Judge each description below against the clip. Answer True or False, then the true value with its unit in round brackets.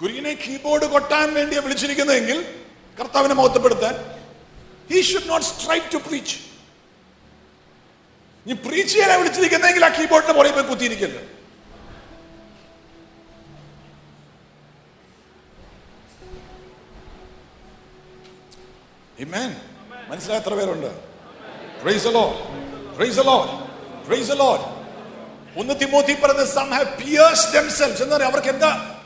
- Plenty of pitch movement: False (3.2 semitones)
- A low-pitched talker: False (280 Hz)